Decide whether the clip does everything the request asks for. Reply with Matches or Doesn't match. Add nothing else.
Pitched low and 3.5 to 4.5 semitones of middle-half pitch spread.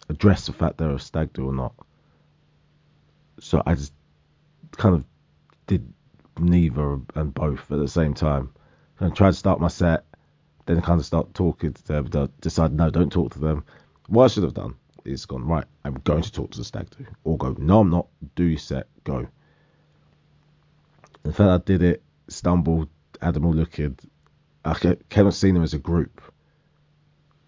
Matches